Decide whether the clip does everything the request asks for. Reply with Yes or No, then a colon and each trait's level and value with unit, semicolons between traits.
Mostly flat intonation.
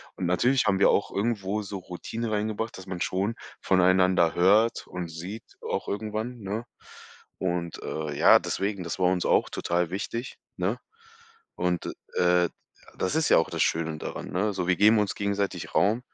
No: average, 3.3 semitones